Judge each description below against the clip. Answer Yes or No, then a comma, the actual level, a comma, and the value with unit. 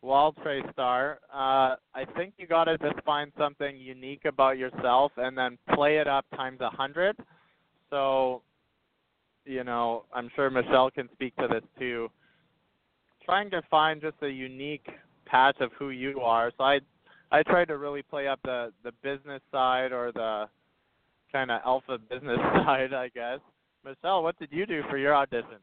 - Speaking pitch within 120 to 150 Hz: Yes, low, 135 Hz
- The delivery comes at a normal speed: Yes, average, 170 wpm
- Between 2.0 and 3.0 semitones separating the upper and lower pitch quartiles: Yes, narrow, 2.6 semitones